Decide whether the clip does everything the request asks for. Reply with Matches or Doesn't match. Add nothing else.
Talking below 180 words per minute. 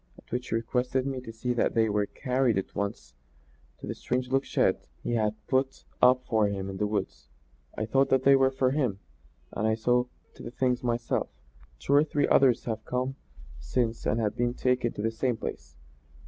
Doesn't match